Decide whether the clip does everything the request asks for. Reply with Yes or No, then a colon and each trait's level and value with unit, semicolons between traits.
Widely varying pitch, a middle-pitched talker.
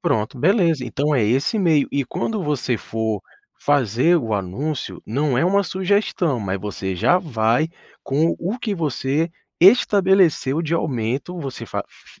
Yes: wide, 6.6 semitones; medium, 145 Hz